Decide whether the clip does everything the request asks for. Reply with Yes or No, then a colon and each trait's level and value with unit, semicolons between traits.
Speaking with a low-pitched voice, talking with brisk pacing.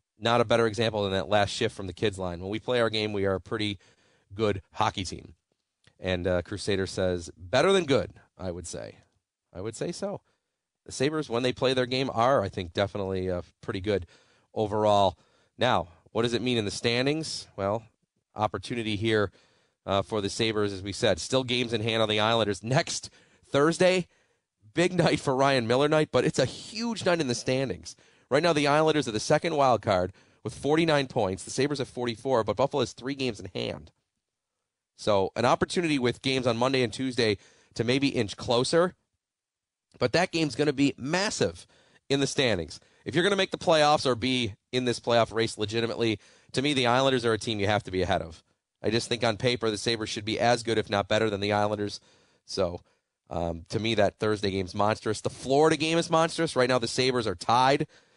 Yes: low, 115 Hz; fast, 210 wpm